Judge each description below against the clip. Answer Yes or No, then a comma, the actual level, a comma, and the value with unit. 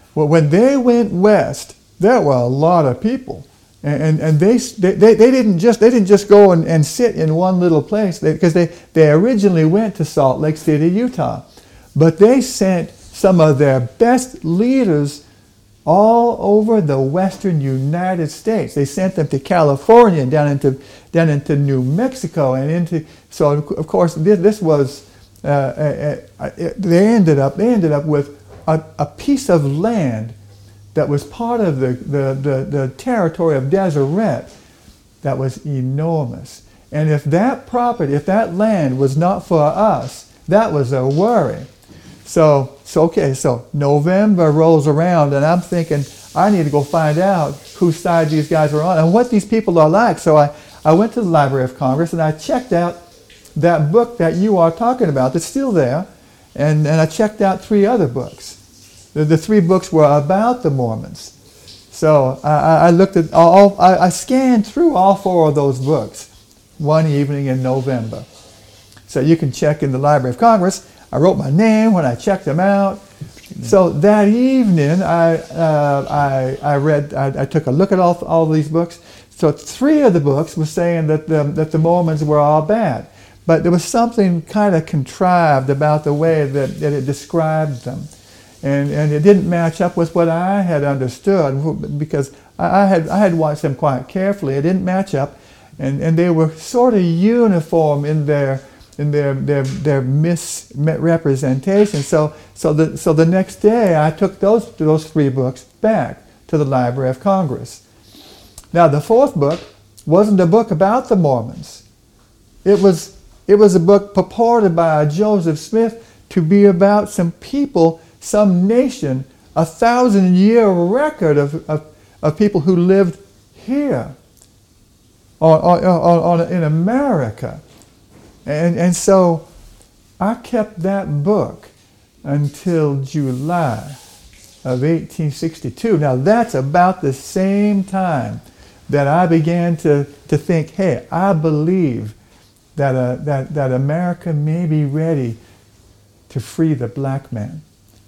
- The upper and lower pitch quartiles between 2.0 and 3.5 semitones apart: No, average, 5.1 semitones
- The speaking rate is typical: Yes, average, 165 wpm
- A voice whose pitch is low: No, medium, 160 Hz